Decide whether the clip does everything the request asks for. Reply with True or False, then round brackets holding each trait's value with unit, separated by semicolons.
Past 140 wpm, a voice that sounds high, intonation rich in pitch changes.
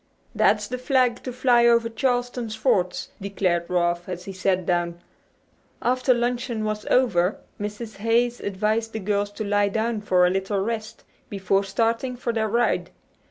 False (160 wpm; 215 Hz; 3.5 semitones)